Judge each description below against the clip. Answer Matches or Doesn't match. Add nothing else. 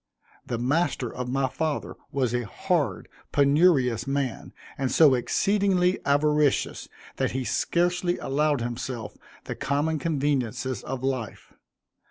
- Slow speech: Matches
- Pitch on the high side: Doesn't match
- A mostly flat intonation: Doesn't match